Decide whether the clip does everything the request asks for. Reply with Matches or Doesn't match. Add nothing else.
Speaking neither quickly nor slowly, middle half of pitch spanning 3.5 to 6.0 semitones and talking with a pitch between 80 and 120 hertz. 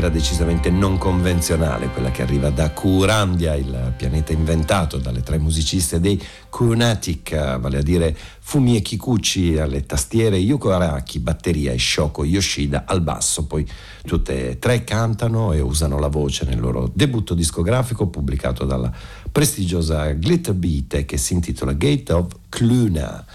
Matches